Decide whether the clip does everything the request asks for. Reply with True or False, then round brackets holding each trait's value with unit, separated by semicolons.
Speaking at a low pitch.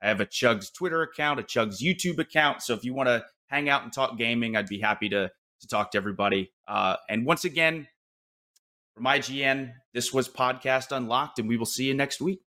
True (130 Hz)